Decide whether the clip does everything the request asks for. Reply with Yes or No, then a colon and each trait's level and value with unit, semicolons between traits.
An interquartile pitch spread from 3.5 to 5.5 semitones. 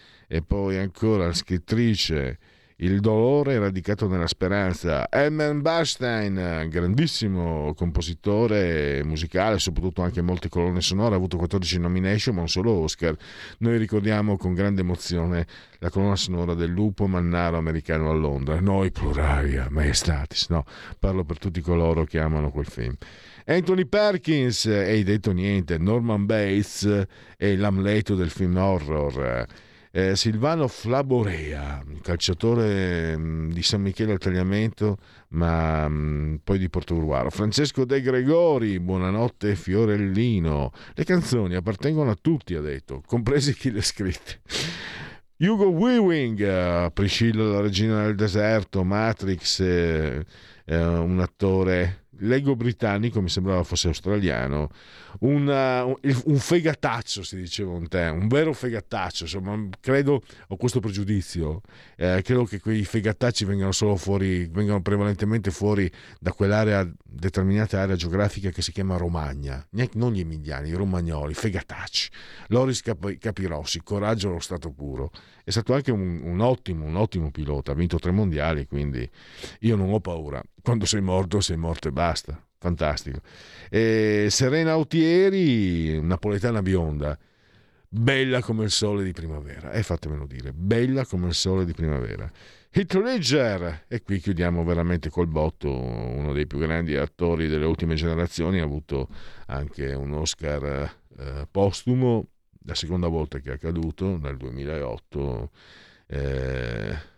Yes: average, 4.8 semitones